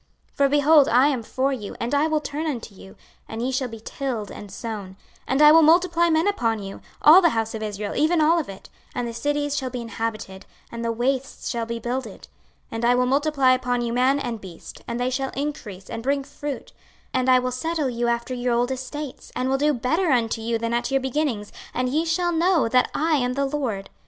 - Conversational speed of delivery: No, fast, 235 wpm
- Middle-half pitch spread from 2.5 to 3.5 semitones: No, average, 4.0 semitones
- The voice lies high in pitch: Yes, very high, 255 Hz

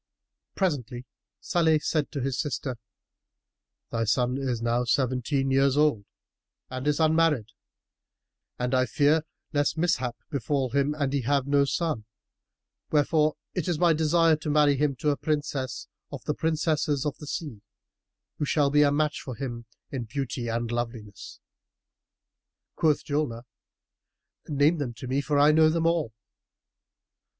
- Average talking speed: Yes, average, 150 wpm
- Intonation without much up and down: No, average, 3.4 semitones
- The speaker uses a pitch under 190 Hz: Yes, medium, 140 Hz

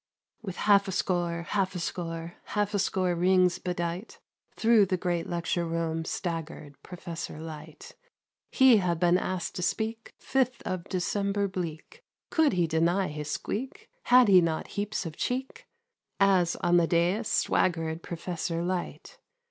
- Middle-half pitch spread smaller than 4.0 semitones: Yes, average, 3.1 semitones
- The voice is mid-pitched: Yes, medium, 180 Hz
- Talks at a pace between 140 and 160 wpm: Yes, average, 150 wpm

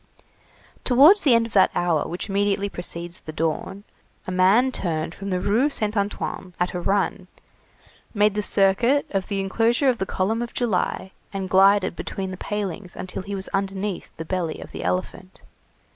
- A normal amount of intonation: No, narrow, 2.3 semitones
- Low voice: No, high, 195 Hz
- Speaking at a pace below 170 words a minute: No, average, 175 wpm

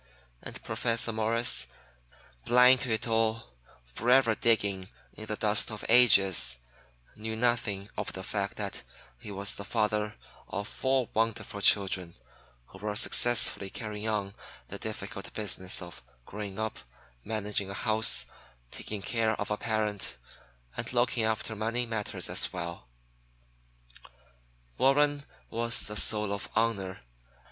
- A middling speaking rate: No, slow, 130 wpm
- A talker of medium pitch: No, low, 110 Hz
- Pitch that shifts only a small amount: Yes, narrow, 2.3 semitones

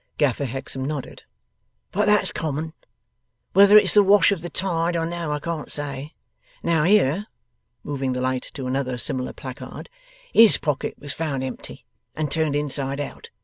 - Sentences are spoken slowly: No, average, 160 wpm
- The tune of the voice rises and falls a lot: No, average, 4.0 semitones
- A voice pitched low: No, medium, 150 Hz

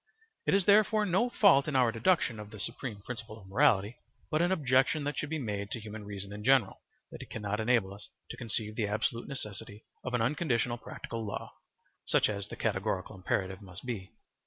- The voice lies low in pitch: Yes, low, 115 Hz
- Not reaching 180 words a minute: No, average, 200 wpm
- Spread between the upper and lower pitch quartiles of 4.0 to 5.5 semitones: Yes, average, 4.7 semitones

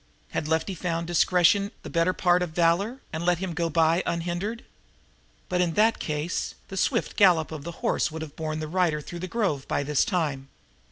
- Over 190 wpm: Yes, average, 200 wpm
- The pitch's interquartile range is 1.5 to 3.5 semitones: Yes, narrow, 2.4 semitones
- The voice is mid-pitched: Yes, medium, 170 Hz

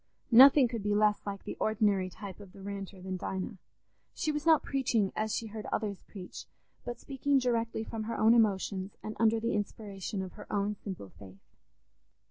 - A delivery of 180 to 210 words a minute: Yes, average, 185 wpm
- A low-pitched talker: No, high, 210 Hz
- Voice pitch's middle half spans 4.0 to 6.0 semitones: No, average, 2.8 semitones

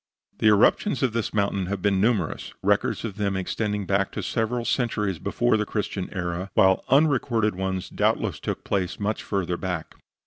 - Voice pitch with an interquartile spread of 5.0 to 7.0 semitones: No, average, 2.9 semitones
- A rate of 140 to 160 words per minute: No, average, 170 wpm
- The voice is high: No, low, 100 Hz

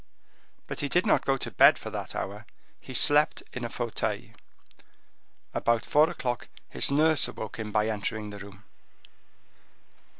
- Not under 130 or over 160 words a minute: Yes, average, 155 wpm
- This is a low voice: Yes, low, 120 Hz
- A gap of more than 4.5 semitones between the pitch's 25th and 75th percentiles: Yes, average, 5.2 semitones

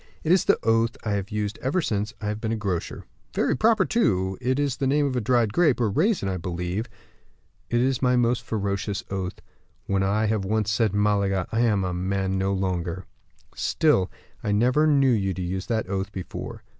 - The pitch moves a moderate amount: Yes, average, 4.2 semitones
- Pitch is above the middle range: No, low, 105 Hz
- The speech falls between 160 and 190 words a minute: No, average, 200 wpm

